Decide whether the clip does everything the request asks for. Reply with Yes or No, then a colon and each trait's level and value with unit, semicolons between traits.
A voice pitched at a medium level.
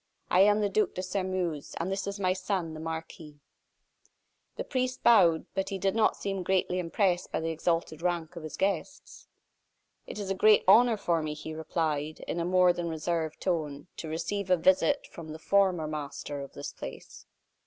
Yes: medium, 175 Hz